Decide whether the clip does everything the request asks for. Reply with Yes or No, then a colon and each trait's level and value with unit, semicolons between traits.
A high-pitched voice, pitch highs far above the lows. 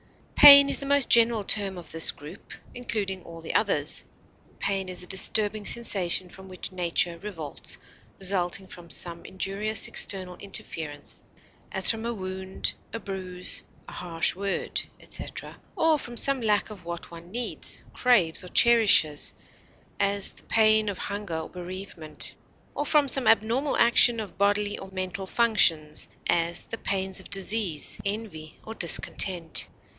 No: high, 195 Hz; average, 3.8 semitones